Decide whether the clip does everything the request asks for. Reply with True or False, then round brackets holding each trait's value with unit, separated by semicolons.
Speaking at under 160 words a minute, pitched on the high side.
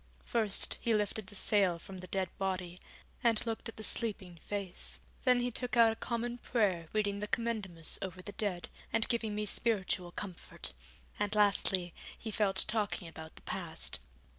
False (175 wpm; 205 Hz)